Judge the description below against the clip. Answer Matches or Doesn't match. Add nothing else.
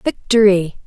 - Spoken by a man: Doesn't match